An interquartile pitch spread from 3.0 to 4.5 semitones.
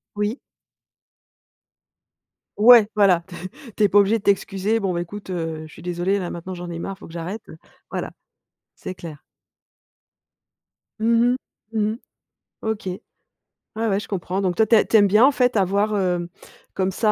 Yes: average, 3.4 semitones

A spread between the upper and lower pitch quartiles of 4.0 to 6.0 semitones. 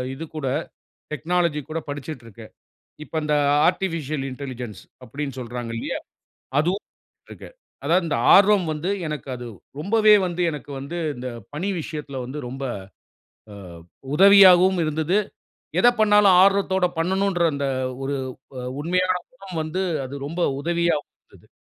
Yes: average, 4.7 semitones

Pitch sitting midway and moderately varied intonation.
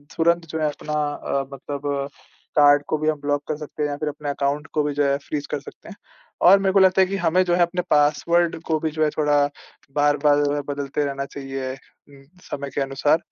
No: medium, 145 Hz; narrow, 1.9 semitones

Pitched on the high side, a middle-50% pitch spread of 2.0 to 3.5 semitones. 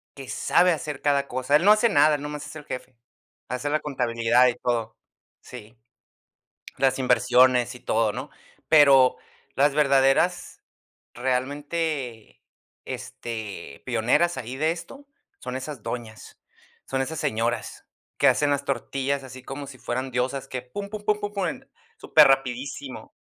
No: low, 135 Hz; average, 3.0 semitones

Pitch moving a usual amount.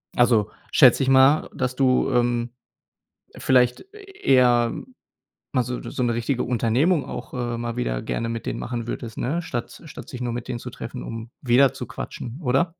No: narrow, 2.0 semitones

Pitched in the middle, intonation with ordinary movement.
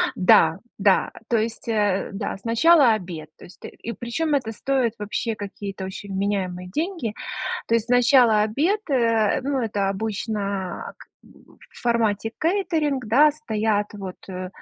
No: high, 220 Hz; average, 4.0 semitones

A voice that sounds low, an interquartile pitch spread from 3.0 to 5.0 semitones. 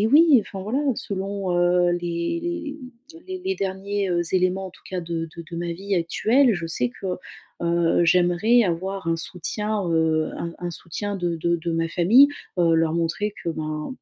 No: medium, 175 Hz; average, 3.4 semitones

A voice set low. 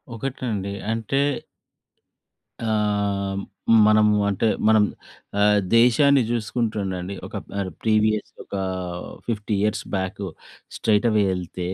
Yes: low, 105 Hz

